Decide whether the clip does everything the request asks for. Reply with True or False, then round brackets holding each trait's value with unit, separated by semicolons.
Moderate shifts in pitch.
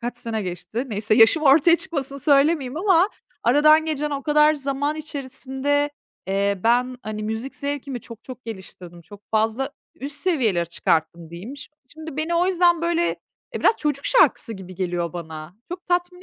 False (6.2 semitones)